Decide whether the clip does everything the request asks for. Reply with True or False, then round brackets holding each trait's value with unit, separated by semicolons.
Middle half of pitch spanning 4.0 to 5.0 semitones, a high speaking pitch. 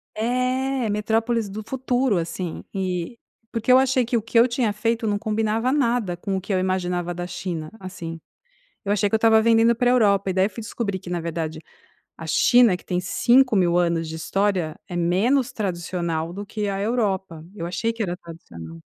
True (4.6 semitones; 205 Hz)